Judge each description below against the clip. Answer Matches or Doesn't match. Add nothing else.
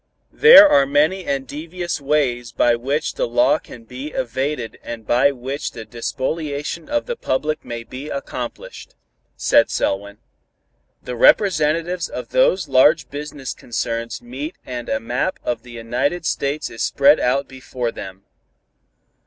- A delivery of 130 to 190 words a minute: Matches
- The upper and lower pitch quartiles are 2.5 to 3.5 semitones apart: Doesn't match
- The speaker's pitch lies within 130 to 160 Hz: Matches